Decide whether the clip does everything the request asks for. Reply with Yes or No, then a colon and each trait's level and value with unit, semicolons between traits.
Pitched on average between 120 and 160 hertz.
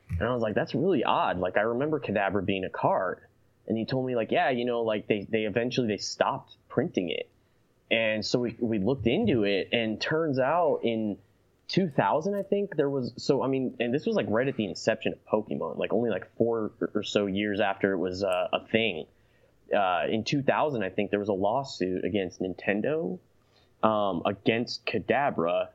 No: low, 110 Hz